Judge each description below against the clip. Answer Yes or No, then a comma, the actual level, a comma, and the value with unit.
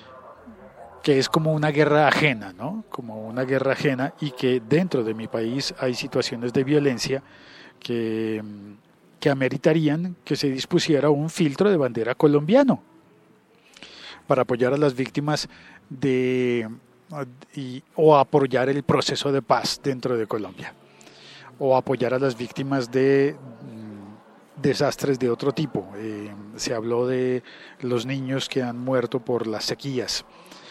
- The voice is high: No, low, 135 Hz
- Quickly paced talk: No, average, 135 wpm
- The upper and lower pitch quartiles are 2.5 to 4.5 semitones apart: Yes, average, 3.2 semitones